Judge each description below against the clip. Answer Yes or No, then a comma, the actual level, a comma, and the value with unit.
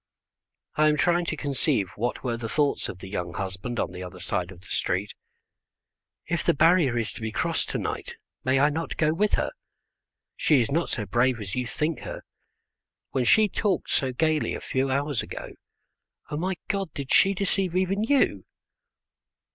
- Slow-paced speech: No, average, 185 wpm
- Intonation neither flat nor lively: No, wide, 6.9 semitones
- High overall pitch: No, medium, 140 Hz